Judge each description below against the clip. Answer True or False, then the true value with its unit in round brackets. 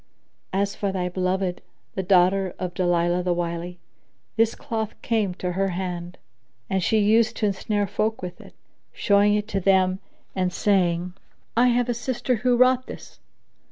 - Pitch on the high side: True (195 Hz)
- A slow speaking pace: False (160 wpm)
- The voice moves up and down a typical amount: True (3.3 semitones)